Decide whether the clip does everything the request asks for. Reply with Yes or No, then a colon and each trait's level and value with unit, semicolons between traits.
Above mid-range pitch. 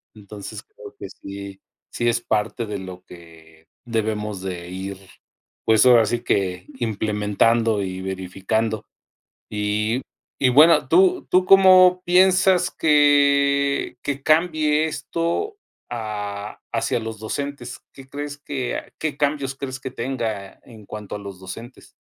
No: low, 115 Hz